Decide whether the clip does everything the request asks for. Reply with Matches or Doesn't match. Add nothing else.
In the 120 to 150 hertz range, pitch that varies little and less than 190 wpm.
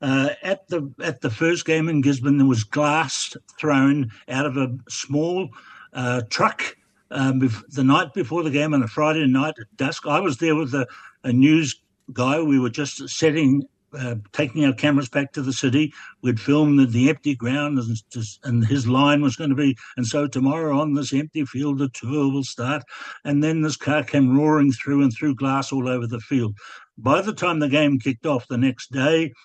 Doesn't match